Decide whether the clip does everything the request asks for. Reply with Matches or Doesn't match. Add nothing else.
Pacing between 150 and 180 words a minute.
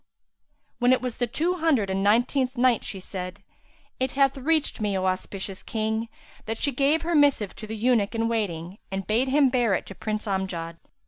Doesn't match